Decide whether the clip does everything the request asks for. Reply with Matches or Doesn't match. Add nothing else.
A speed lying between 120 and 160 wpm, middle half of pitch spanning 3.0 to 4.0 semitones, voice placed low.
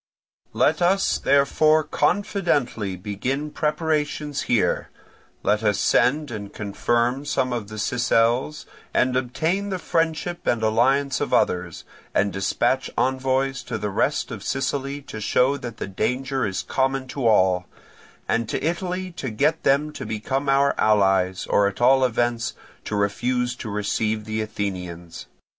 Doesn't match